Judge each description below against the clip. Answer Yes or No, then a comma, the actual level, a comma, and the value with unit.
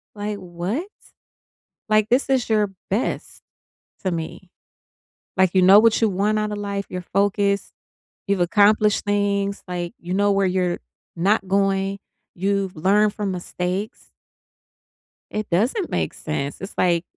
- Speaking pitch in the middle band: No, high, 200 Hz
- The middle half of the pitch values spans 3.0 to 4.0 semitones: No, narrow, 2.4 semitones